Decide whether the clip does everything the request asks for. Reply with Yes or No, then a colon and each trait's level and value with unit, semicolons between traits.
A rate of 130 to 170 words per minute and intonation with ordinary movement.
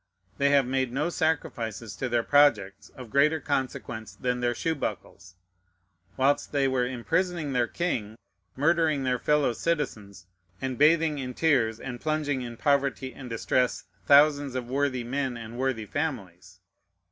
Yes: average, 145 wpm; average, 3.5 semitones